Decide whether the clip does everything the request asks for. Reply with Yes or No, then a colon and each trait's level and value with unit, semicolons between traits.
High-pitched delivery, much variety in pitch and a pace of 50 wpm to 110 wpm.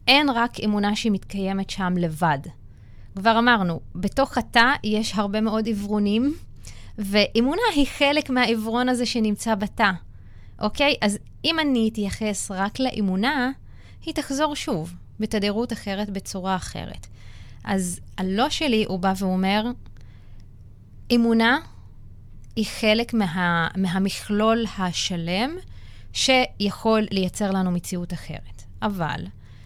No: high, 205 Hz; average, 5.0 semitones; average, 105 wpm